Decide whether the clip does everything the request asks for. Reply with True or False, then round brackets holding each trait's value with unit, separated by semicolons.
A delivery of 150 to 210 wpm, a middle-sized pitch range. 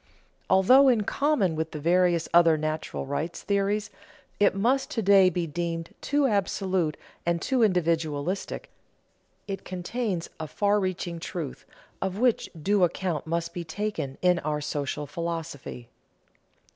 False (135 wpm; 3.9 semitones)